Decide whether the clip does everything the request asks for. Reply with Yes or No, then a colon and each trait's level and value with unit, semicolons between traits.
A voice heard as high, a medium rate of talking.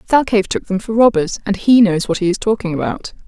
No: high, 205 Hz; fast, 240 wpm